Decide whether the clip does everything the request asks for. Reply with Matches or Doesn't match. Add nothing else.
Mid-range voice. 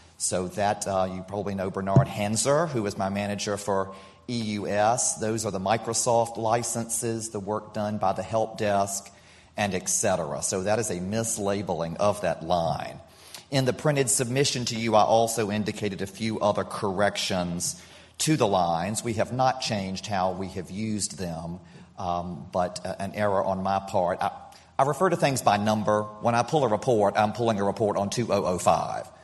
Doesn't match